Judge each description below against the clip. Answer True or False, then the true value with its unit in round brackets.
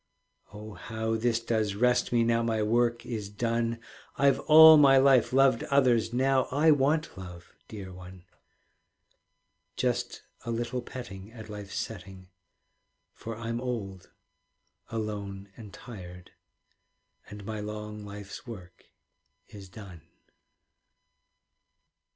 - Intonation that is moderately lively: True (3.2 semitones)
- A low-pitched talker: True (110 Hz)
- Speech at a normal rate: False (115 wpm)